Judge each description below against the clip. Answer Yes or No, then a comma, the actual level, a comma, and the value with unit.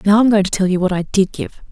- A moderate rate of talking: No, fast, 350 wpm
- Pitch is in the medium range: No, high, 195 Hz